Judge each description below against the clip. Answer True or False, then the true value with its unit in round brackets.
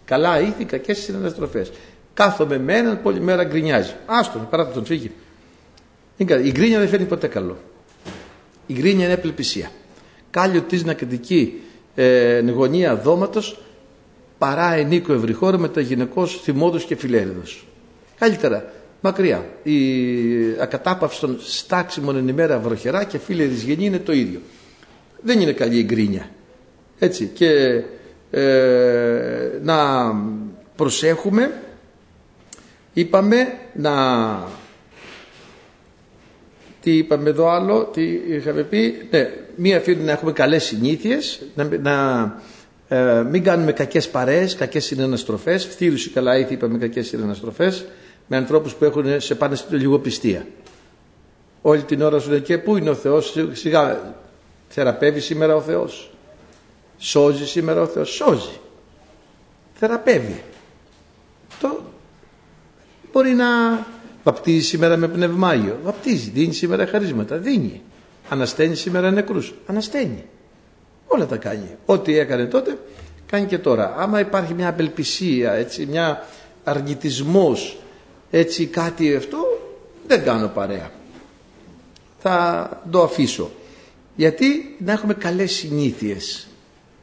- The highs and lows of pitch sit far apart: True (5.8 semitones)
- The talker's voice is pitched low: False (160 Hz)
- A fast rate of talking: False (120 wpm)